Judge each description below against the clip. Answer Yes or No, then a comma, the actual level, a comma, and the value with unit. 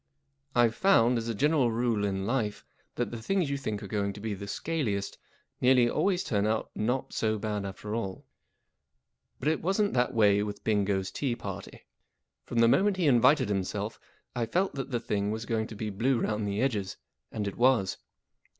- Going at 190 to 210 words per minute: Yes, average, 195 wpm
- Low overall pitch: Yes, low, 110 Hz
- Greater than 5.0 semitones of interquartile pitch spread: No, average, 3.9 semitones